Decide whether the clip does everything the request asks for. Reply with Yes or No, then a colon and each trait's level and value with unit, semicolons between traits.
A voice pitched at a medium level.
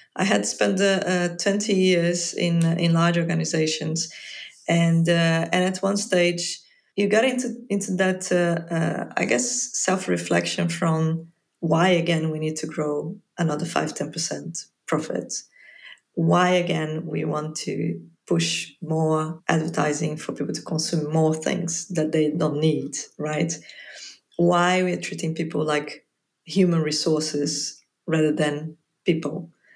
Yes: medium, 165 Hz